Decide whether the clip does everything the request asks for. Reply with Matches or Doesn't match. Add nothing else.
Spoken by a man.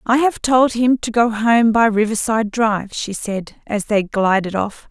Doesn't match